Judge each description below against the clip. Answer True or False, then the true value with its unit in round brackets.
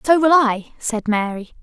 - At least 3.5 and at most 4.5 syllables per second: True (4.4 syllables/s)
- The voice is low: False (245 Hz)